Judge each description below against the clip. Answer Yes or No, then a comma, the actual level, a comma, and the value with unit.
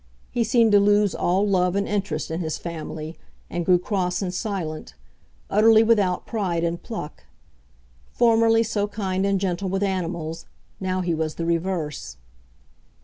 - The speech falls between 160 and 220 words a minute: No, average, 150 wpm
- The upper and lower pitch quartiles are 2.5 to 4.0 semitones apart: Yes, average, 3.5 semitones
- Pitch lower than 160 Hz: No, medium, 185 Hz